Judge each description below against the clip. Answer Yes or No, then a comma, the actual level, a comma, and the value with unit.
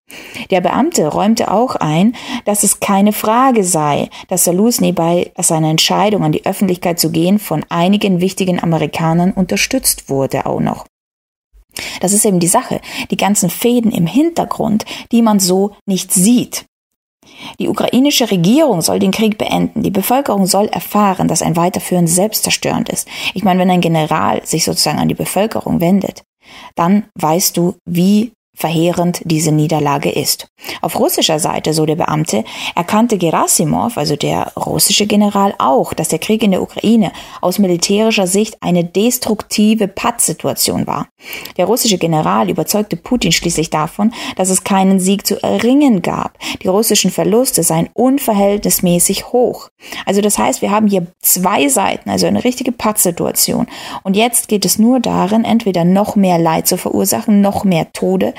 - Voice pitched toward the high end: Yes, high, 195 Hz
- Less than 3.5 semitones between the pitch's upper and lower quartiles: No, average, 3.8 semitones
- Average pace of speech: Yes, average, 155 wpm